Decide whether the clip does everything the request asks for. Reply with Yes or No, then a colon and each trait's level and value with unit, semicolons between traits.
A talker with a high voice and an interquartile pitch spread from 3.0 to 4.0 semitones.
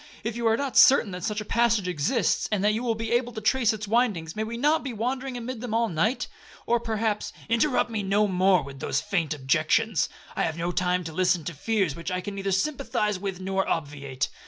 No: high, 210 Hz; average, 4.4 semitones